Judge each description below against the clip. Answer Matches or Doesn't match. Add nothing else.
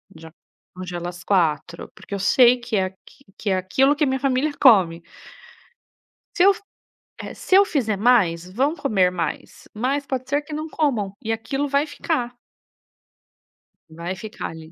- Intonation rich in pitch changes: Matches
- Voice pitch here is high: Matches